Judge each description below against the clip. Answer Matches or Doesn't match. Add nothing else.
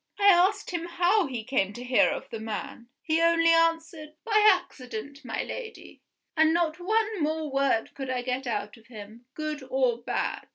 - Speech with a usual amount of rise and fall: Doesn't match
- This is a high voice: Matches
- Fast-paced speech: Doesn't match